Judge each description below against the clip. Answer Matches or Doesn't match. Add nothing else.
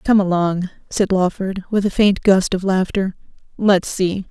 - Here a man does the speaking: Doesn't match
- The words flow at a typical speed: Matches